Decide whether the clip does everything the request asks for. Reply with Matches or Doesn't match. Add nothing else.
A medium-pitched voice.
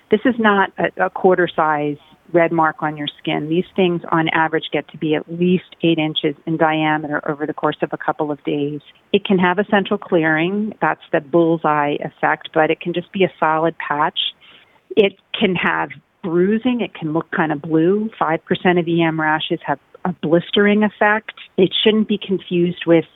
Matches